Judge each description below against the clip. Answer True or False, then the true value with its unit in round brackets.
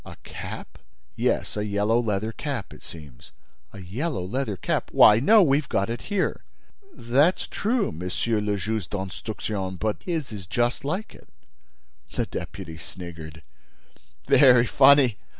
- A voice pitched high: False (110 Hz)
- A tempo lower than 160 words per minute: True (140 wpm)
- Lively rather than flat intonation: True (6.3 semitones)